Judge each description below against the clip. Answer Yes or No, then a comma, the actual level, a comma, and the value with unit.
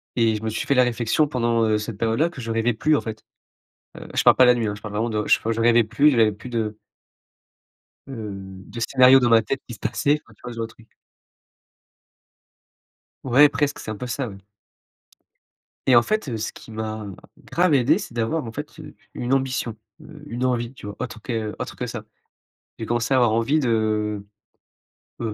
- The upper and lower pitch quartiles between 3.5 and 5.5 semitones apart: No, average, 2.7 semitones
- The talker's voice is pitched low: Yes, low, 115 Hz